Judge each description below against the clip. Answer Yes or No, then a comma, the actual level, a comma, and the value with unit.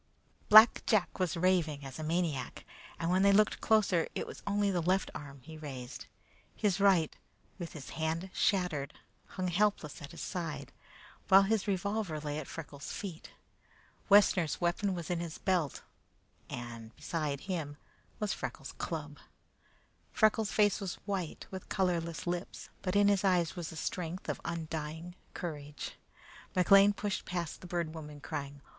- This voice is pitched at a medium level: Yes, medium, 175 Hz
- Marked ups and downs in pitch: No, average, 4.0 semitones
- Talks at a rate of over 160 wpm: No, average, 155 wpm